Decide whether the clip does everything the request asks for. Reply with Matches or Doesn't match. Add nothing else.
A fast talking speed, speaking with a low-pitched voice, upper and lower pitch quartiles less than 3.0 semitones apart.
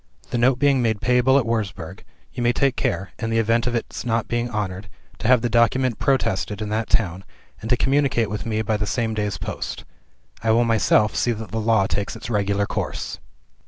Matches